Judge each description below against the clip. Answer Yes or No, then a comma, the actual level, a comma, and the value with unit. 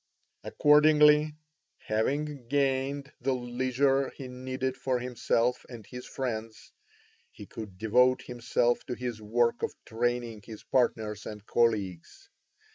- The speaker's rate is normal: No, slow, 120 wpm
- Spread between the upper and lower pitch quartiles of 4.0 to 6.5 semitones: No, average, 2.8 semitones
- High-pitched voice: No, low, 125 Hz